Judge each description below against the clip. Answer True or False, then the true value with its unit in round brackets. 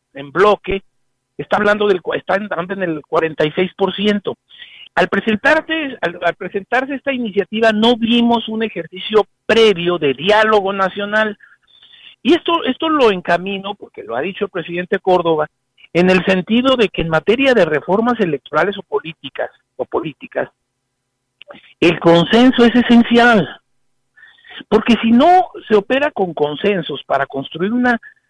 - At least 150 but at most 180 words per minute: False (140 wpm)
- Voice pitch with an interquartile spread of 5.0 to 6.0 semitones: True (5.6 semitones)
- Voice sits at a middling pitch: False (200 Hz)